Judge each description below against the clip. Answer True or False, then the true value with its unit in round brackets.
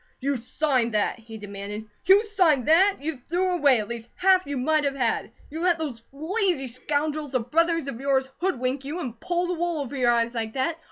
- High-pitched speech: True (280 Hz)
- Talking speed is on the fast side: True (210 wpm)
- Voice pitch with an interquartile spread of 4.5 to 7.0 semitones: True (5.5 semitones)